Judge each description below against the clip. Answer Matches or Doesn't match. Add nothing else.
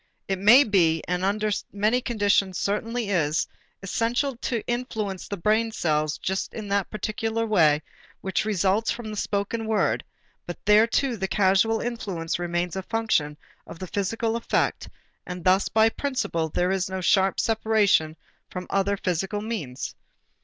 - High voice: Matches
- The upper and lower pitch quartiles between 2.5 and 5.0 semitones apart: Matches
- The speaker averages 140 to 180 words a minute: Matches